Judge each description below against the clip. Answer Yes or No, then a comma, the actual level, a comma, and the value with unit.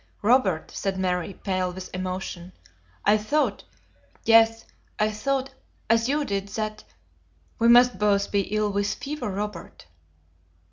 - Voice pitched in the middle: No, high, 210 Hz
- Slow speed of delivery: Yes, slow, 130 wpm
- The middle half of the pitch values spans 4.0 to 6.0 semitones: No, average, 3.2 semitones